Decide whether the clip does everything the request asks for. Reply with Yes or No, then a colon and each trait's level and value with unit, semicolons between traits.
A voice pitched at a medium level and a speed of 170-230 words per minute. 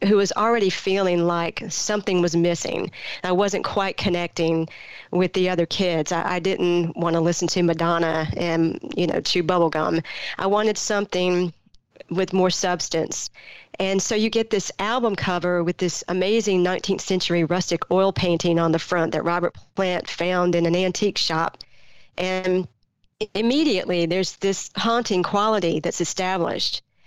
No: medium, 180 Hz; average, 155 wpm